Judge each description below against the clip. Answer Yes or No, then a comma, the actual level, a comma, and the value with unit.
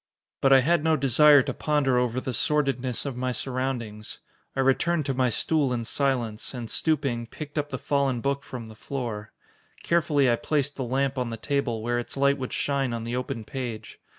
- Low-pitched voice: Yes, low, 130 Hz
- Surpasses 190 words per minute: Yes, average, 200 wpm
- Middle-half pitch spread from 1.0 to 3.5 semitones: Yes, average, 2.8 semitones